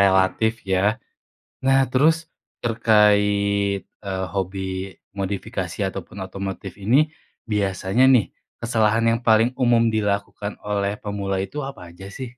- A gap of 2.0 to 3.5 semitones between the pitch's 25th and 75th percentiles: Yes, narrow, 2.6 semitones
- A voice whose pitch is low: Yes, low, 100 Hz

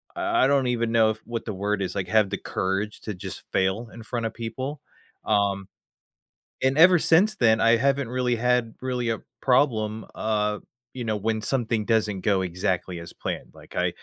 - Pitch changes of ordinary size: Yes, average, 3.0 semitones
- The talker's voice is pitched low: Yes, low, 115 Hz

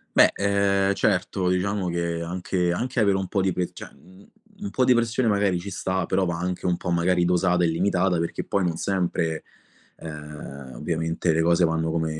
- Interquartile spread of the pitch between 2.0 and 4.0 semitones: Yes, narrow, 2.6 semitones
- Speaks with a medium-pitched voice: No, very low, 90 Hz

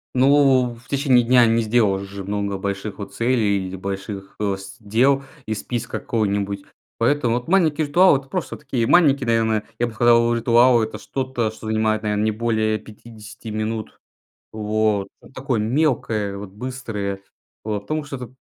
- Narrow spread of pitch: No, average, 3.5 semitones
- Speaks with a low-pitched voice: Yes, low, 115 Hz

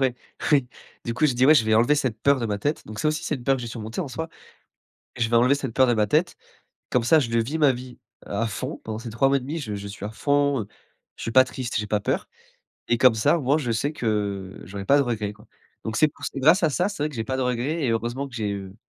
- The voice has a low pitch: Yes, low, 125 Hz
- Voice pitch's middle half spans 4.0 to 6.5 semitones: Yes, average, 4.3 semitones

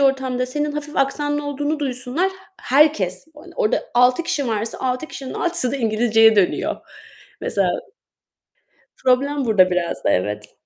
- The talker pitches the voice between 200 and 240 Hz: No, very high, 255 Hz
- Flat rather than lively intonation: No, average, 4.8 semitones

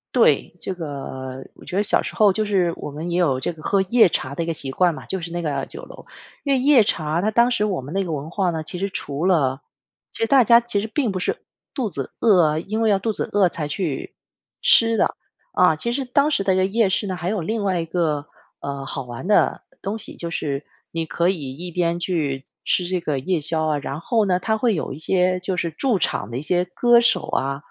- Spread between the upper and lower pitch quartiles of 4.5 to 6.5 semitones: Yes, average, 5.0 semitones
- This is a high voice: No, medium, 180 Hz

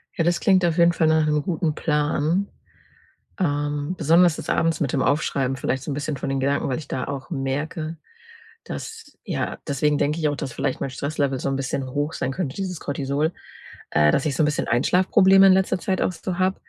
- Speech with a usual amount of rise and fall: Yes, average, 3.7 semitones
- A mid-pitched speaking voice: Yes, medium, 150 Hz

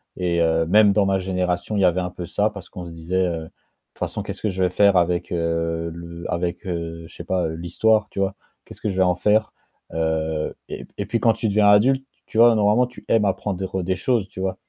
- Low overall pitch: Yes, very low, 95 Hz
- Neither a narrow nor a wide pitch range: Yes, average, 3.4 semitones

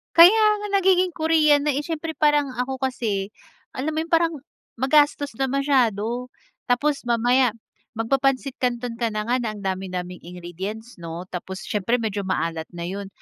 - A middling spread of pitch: No, wide, 6.6 semitones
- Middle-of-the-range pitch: No, very high, 250 Hz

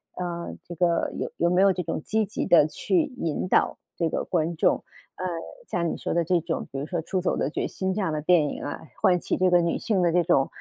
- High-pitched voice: No, medium, 175 Hz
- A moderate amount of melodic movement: No, narrow, 2.0 semitones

